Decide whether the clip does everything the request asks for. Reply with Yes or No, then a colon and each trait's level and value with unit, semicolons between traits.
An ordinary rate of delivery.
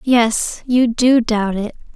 Yes: average, 155 wpm